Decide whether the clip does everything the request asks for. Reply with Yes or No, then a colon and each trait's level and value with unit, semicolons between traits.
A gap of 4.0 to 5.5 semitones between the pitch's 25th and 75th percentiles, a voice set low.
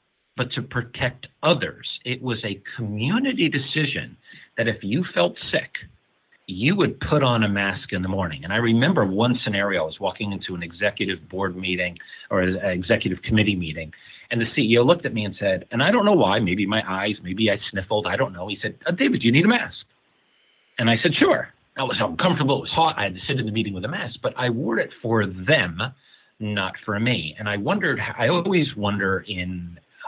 Yes: average, 4.6 semitones; low, 110 Hz